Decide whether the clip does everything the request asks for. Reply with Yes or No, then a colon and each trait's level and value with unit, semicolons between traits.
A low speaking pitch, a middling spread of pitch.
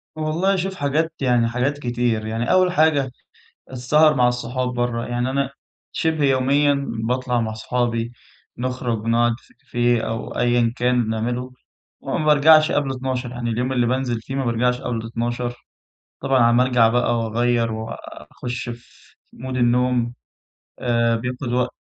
No: low, 125 Hz; narrow, 2.0 semitones